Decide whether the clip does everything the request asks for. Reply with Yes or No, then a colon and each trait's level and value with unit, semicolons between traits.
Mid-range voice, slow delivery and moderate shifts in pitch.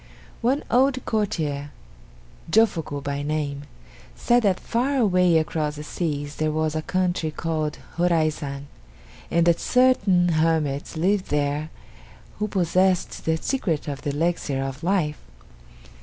Yes: medium, 160 Hz; slow, 125 wpm; average, 4.0 semitones